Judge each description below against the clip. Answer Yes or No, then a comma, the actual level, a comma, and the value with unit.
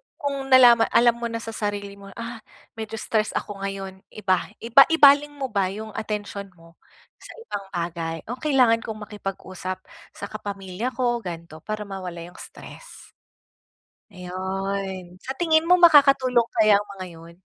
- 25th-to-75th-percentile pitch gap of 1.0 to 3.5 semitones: No, average, 4.2 semitones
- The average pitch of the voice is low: No, high, 210 Hz